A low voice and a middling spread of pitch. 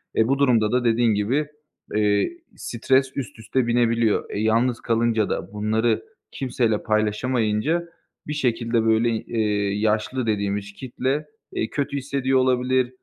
Yes: low, 115 Hz; average, 3.2 semitones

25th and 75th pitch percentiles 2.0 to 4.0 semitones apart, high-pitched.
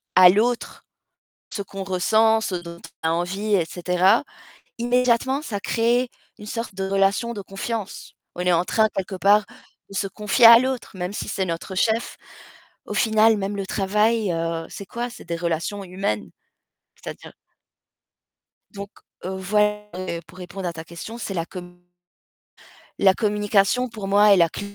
Yes: average, 3.4 semitones; high, 200 Hz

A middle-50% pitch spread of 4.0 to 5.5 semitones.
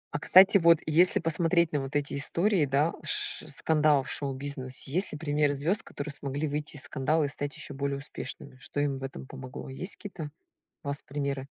No: narrow, 2.6 semitones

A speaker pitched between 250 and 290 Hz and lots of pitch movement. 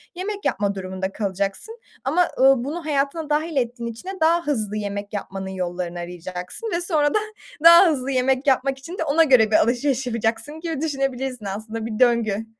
Yes: very high, 255 Hz; wide, 6.7 semitones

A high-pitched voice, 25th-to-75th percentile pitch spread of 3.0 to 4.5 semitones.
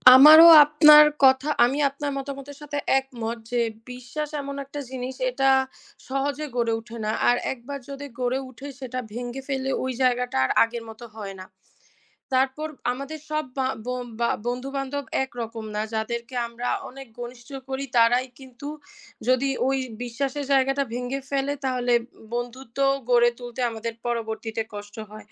No: very high, 255 Hz; narrow, 2.4 semitones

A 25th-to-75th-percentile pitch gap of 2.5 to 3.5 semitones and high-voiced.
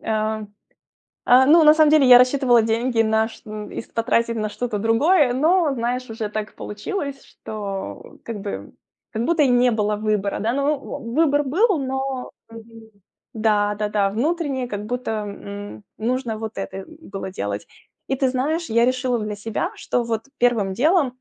No: average, 4.0 semitones; high, 235 Hz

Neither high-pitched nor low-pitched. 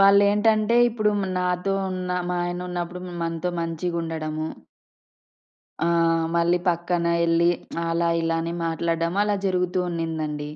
Yes: medium, 175 Hz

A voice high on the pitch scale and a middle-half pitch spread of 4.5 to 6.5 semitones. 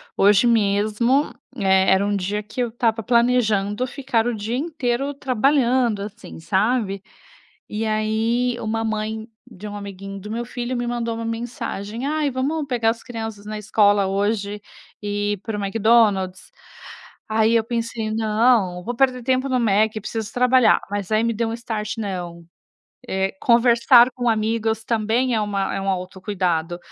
No: high, 220 Hz; average, 2.8 semitones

